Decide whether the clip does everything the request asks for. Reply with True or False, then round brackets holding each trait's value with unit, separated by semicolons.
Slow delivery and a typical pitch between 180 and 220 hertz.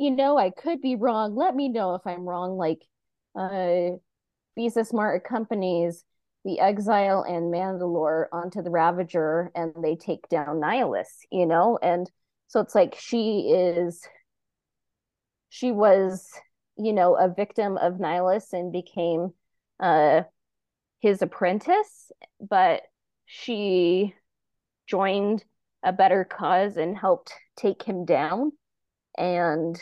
True (125 wpm; 185 Hz)